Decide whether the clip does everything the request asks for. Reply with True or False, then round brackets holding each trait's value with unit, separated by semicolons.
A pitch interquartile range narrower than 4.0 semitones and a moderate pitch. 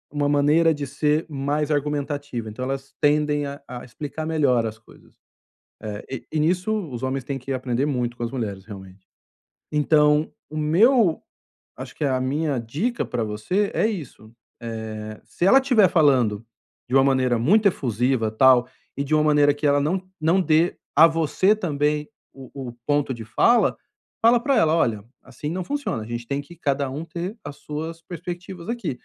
False (4.4 semitones; 145 Hz)